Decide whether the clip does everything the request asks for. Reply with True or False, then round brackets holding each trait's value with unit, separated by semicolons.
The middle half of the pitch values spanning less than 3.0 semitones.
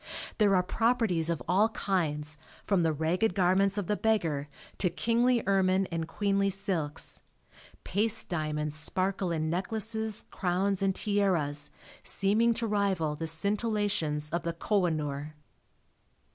False (4.3 semitones)